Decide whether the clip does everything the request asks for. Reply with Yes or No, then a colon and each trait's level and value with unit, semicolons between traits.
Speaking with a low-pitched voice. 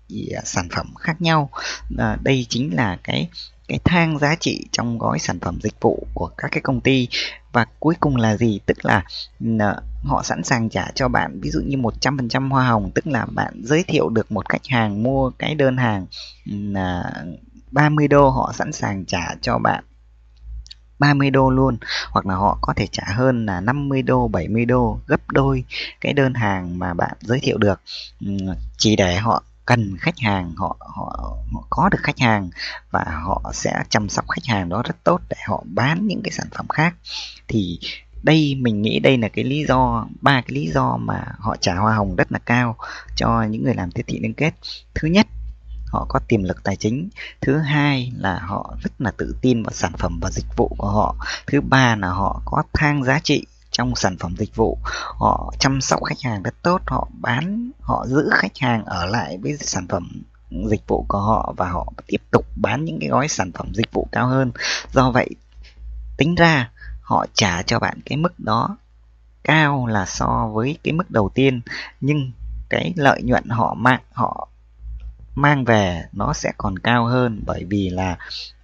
Yes: low, 115 Hz